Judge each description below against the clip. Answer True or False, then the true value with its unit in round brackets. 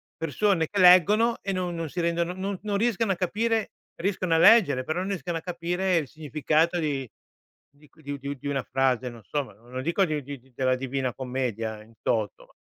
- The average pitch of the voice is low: False (160 Hz)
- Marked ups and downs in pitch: True (5.7 semitones)